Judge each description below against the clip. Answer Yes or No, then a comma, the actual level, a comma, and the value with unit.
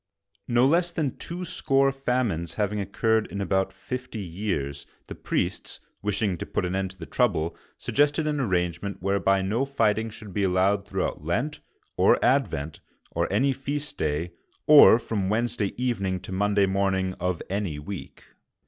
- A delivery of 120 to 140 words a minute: No, average, 155 wpm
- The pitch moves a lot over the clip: No, average, 5.0 semitones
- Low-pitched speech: Yes, low, 100 Hz